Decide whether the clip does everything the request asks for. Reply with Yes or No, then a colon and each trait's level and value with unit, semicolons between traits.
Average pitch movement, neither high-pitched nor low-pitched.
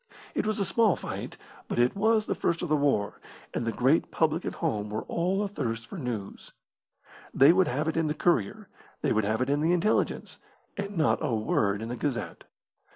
No: wide, 7.4 semitones; medium, 150 Hz